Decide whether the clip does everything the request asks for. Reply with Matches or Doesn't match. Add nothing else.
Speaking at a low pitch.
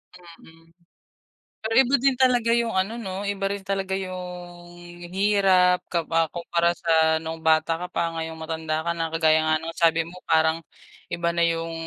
Doesn't match